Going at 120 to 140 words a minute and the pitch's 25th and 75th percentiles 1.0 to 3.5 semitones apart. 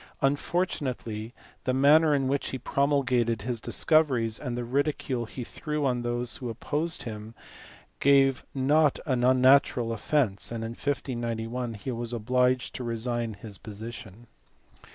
Yes: slow, 135 wpm; average, 3.2 semitones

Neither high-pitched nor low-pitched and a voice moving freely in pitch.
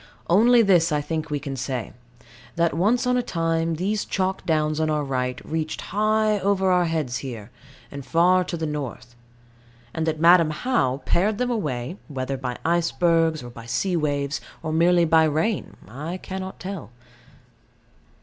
No: medium, 165 Hz; average, 4.5 semitones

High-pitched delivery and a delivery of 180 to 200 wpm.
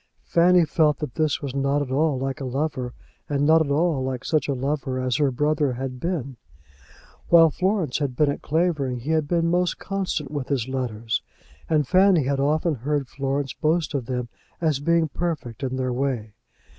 No: medium, 145 Hz; average, 190 wpm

